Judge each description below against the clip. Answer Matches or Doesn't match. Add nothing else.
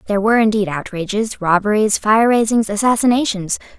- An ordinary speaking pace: Doesn't match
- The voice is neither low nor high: Doesn't match